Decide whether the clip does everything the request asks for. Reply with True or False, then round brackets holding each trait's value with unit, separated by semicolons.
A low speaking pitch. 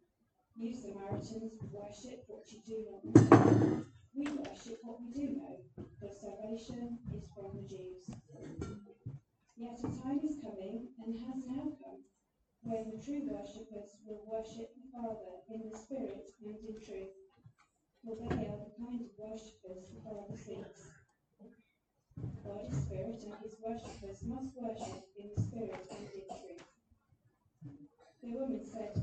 False (220 Hz)